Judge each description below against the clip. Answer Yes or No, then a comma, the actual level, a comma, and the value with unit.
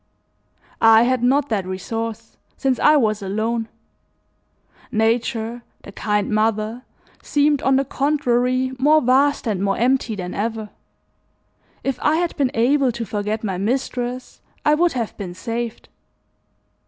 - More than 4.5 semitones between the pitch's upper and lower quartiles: No, average, 3.5 semitones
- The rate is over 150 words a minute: No, slow, 135 wpm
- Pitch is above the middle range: Yes, high, 235 Hz